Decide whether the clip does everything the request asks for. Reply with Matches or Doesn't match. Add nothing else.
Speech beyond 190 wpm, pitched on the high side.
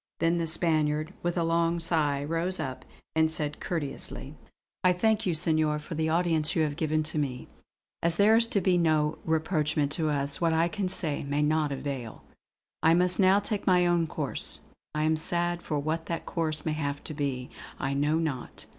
Doesn't match